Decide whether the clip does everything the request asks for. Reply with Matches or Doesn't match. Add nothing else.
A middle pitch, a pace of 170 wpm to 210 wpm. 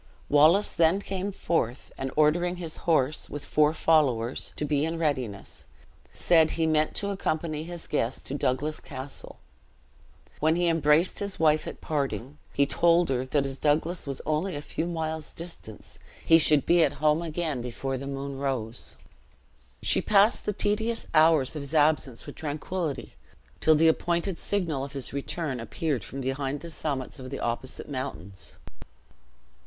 Doesn't match